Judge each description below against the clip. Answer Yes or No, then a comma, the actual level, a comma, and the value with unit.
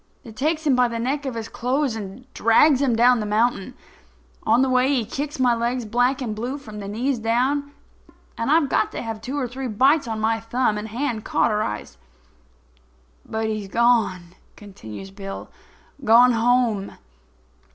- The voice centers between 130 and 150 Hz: No, high, 235 Hz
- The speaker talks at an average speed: Yes, average, 165 wpm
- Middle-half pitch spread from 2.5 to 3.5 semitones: Yes, average, 3.2 semitones